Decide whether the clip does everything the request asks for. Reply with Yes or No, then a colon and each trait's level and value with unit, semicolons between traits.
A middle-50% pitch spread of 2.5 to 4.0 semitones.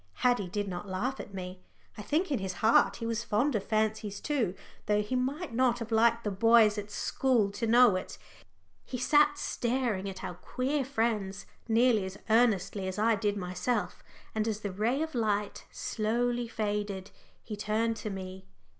Yes: average, 3.4 semitones